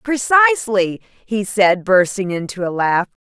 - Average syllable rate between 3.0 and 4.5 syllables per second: Yes, 4.1 syllables/s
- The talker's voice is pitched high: Yes, high, 210 Hz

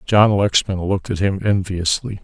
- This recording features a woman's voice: No, male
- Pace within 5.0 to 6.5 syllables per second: No, 4.8 syllables/s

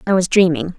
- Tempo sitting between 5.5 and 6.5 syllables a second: Yes, 6.2 syllables/s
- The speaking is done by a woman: Yes, female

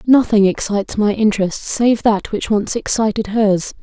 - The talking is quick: No, average, 155 wpm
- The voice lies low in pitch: No, high, 215 Hz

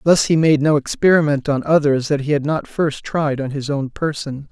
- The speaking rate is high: Yes, fast, 225 wpm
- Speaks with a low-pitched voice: No, medium, 145 Hz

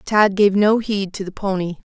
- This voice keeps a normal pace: No, fast, 220 wpm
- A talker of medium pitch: No, high, 200 Hz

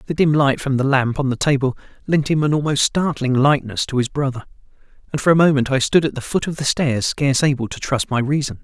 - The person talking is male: Yes, male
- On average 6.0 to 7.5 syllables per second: Yes, 6.1 syllables/s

